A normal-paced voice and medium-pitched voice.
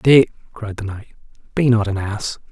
No: average, 190 wpm; low, 110 Hz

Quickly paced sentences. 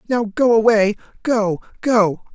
No: slow, 100 wpm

